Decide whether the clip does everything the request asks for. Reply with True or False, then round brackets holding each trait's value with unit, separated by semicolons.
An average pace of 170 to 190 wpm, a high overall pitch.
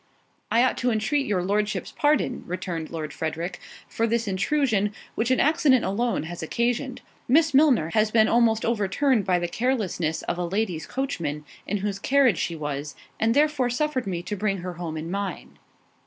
True (175 wpm; 210 Hz)